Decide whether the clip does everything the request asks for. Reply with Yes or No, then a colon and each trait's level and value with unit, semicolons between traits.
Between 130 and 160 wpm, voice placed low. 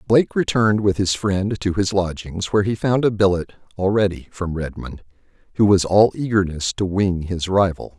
No: average, 180 wpm; low, 100 Hz